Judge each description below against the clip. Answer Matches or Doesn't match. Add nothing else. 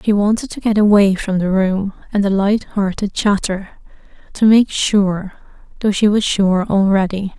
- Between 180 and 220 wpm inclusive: Doesn't match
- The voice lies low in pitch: Doesn't match